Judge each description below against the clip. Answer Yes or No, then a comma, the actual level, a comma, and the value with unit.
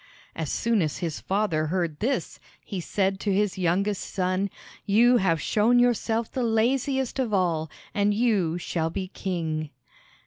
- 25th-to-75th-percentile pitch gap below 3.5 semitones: No, average, 4.6 semitones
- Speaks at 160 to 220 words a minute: No, average, 150 wpm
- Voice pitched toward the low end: No, high, 195 Hz